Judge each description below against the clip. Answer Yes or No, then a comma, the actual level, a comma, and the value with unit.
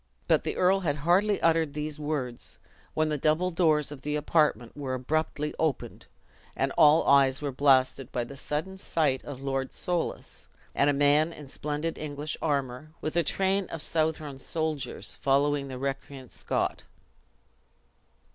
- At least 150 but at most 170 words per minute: Yes, average, 155 wpm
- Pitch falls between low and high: Yes, medium, 150 Hz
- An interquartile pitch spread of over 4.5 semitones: No, narrow, 2.6 semitones